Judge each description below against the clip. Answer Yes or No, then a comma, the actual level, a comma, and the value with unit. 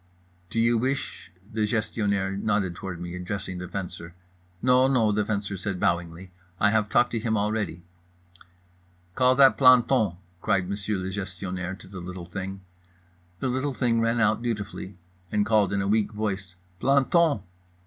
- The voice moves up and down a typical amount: Yes, average, 3.5 semitones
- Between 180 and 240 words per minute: No, average, 155 wpm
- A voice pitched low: Yes, low, 105 Hz